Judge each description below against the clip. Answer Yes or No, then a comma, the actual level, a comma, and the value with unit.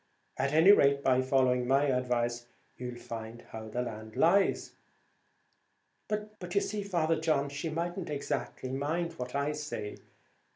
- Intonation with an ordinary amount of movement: Yes, average, 5.0 semitones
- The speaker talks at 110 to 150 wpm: Yes, average, 140 wpm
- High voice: No, medium, 140 Hz